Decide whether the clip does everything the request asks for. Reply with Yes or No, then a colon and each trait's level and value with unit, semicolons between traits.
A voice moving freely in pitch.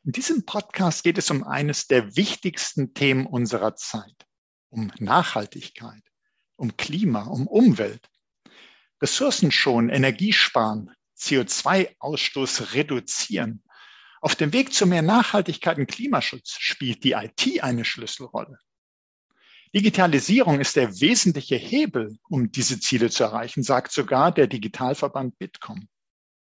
Yes: wide, 8.7 semitones